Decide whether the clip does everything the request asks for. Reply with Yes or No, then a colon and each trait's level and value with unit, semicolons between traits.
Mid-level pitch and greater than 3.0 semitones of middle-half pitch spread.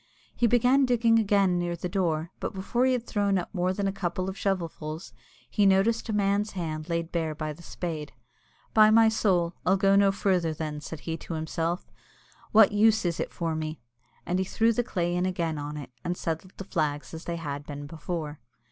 Yes: medium, 180 Hz; average, 3.9 semitones